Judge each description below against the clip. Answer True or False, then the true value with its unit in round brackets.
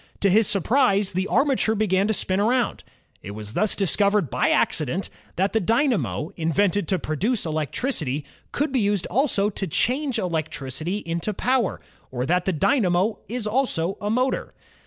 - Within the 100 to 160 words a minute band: True (155 wpm)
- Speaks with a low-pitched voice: False (200 Hz)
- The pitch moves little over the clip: False (5.2 semitones)